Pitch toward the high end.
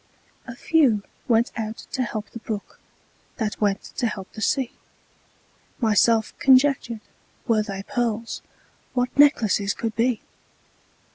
Yes: high, 230 Hz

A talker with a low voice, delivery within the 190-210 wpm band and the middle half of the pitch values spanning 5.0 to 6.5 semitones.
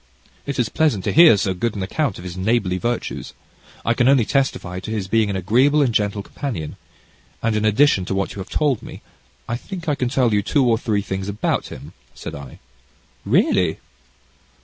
Yes: low, 110 Hz; average, 200 wpm; wide, 5.4 semitones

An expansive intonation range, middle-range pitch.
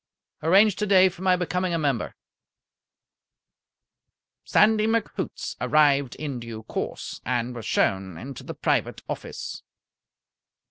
Yes: wide, 7.5 semitones; medium, 155 Hz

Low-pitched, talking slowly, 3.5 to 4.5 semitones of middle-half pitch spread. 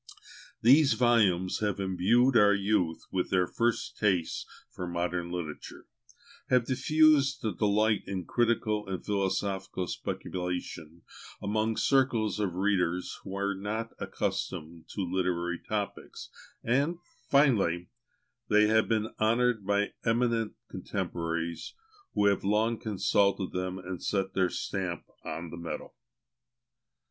Yes: low, 100 Hz; slow, 120 wpm; average, 3.8 semitones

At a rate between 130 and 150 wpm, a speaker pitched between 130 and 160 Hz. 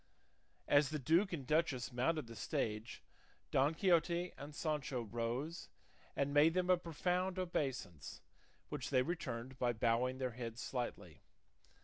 Yes: slow, 135 wpm; medium, 140 Hz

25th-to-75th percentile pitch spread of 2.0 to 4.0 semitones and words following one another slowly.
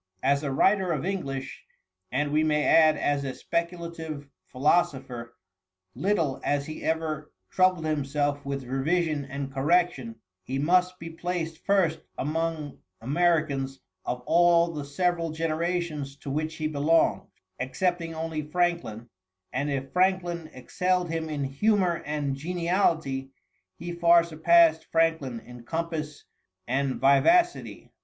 Yes: average, 3.5 semitones; slow, 125 wpm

